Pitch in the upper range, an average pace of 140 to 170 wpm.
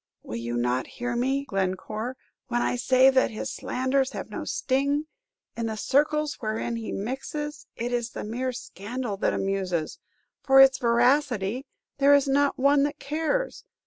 Yes: very high, 255 Hz; average, 160 wpm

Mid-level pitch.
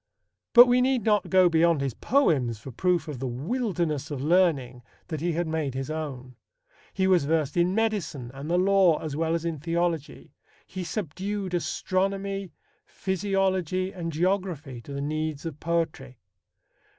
Yes: medium, 170 Hz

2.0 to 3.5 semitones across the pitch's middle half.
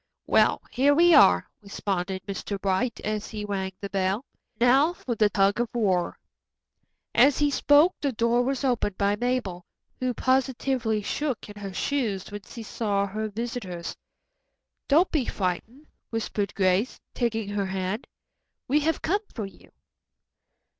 No: average, 4.6 semitones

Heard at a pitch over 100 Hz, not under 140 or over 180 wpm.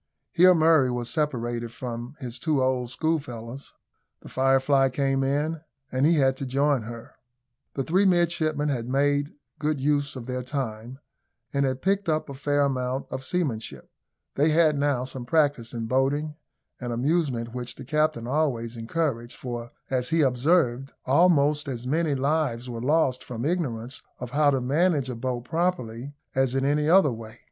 Yes: low, 135 Hz; average, 165 wpm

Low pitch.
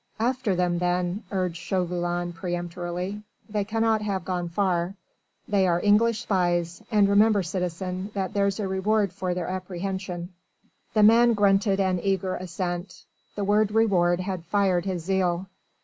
No: high, 190 Hz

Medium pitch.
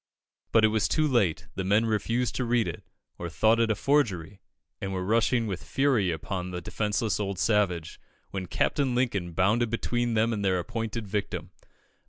No: low, 105 Hz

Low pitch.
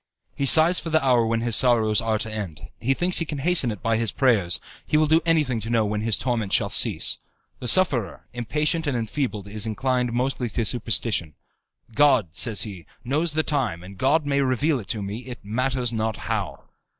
Yes: low, 120 Hz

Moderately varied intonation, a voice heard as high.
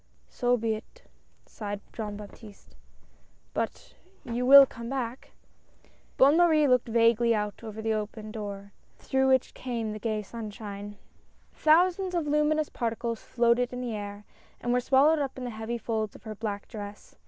Yes: average, 3.6 semitones; high, 230 Hz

